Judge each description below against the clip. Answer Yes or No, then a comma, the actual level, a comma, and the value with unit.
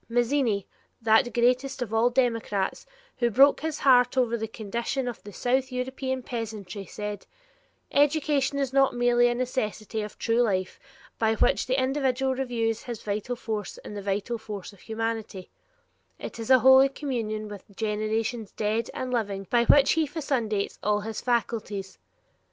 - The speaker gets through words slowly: No, average, 155 wpm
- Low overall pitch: No, high, 235 Hz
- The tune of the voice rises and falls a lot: No, average, 3.3 semitones